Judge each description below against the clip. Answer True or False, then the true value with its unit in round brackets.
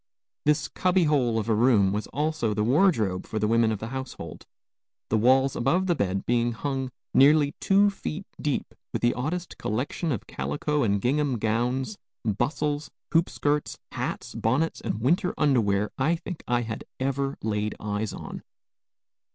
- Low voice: True (130 Hz)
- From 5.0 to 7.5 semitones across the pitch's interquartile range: True (5.3 semitones)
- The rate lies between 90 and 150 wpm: False (160 wpm)